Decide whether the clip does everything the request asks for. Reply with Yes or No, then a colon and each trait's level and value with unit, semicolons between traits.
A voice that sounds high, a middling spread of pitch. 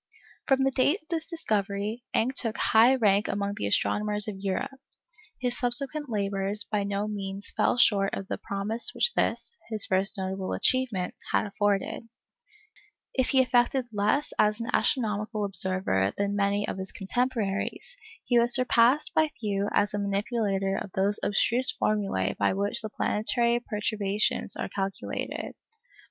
Yes: high, 210 Hz; average, 3.5 semitones